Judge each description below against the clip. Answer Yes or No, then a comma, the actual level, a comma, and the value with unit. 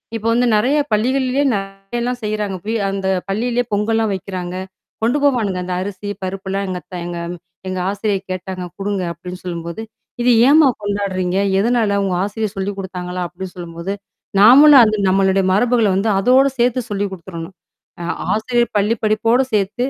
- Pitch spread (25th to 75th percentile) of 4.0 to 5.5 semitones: No, average, 3.5 semitones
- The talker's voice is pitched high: Yes, high, 200 Hz